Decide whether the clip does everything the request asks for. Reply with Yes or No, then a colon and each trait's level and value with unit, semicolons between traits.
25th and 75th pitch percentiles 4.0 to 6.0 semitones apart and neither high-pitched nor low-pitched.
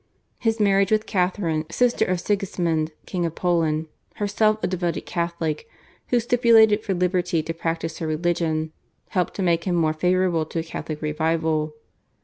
No: average, 3.4 semitones; medium, 175 Hz